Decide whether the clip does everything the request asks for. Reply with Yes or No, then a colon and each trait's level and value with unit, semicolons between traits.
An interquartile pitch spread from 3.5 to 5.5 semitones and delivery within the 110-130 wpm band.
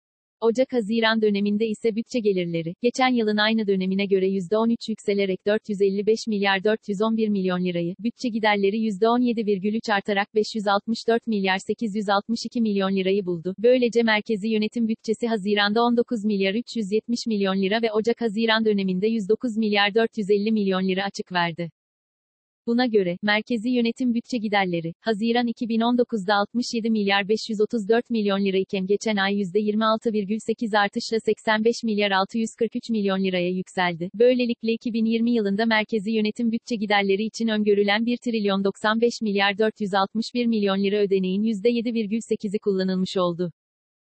No: narrow, 2.4 semitones; average, 125 wpm